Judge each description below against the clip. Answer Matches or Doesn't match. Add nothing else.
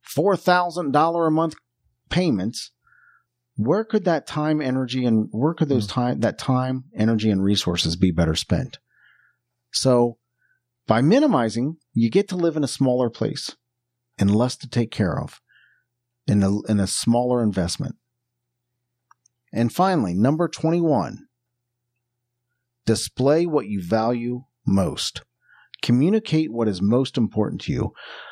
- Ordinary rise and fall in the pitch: Matches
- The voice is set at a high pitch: Doesn't match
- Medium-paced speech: Doesn't match